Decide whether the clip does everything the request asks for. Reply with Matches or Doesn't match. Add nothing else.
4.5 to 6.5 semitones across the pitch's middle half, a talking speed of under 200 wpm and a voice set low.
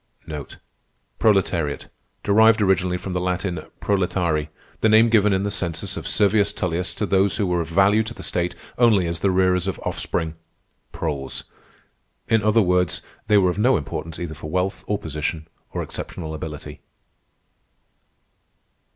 Doesn't match